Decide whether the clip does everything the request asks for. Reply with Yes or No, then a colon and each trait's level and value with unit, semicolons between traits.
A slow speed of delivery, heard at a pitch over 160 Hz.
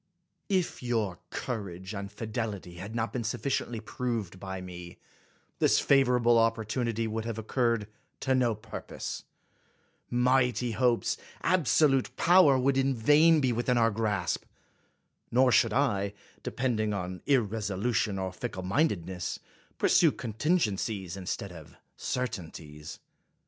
No: slow, 125 wpm; low, 115 Hz